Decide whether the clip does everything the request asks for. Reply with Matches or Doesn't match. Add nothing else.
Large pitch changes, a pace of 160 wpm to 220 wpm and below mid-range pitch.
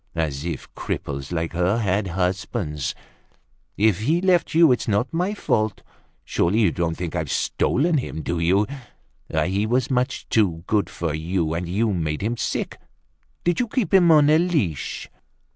Matches